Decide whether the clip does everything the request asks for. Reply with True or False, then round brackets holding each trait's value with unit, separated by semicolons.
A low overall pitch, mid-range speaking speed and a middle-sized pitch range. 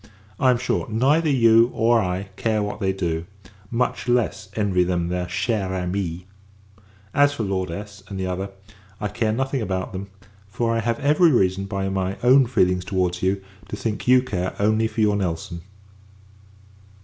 True (100 Hz; 175 wpm; 3.9 semitones)